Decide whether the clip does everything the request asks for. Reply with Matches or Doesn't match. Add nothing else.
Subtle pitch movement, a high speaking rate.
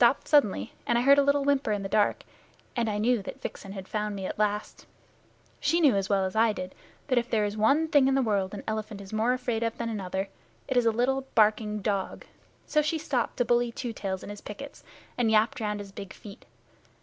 Doesn't match